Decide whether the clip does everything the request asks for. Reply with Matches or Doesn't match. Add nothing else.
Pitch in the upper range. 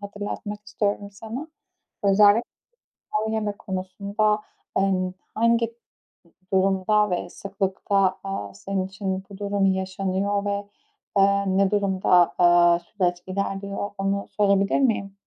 Matches